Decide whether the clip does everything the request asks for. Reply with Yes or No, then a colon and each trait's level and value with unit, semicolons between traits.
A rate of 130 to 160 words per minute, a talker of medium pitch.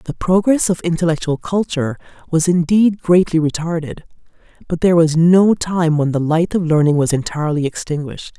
Yes: average, 155 wpm; medium, 165 Hz